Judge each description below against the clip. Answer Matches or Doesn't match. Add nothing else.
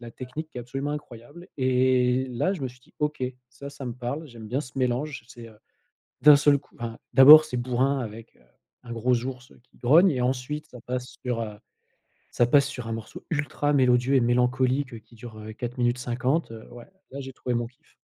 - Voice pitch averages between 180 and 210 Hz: Doesn't match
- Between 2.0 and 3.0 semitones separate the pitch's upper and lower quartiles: Matches